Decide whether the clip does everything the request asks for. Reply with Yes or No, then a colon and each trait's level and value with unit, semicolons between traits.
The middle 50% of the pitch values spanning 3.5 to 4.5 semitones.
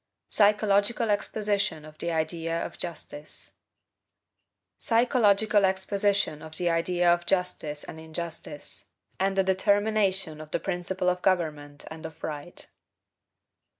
Yes: average, 4.1 semitones